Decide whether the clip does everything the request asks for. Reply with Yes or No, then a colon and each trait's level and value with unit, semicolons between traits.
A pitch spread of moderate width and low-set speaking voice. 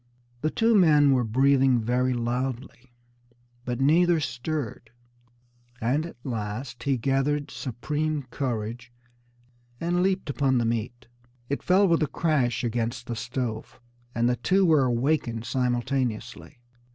Yes: average, 3.7 semitones; low, 130 Hz